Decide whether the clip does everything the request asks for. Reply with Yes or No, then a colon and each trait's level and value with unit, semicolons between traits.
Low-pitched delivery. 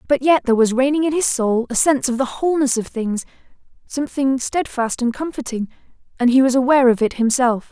No: very high, 260 Hz